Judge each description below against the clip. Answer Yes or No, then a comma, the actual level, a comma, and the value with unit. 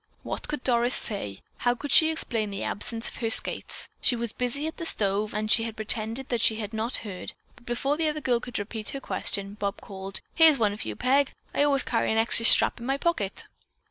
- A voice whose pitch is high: Yes, high, 230 Hz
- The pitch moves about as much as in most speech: Yes, average, 4.1 semitones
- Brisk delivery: Yes, fast, 225 wpm